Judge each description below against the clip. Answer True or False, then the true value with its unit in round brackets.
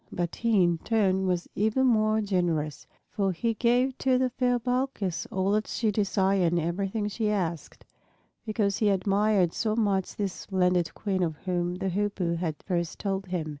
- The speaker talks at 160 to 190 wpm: True (170 wpm)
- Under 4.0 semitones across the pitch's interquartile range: True (3.4 semitones)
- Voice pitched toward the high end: True (195 Hz)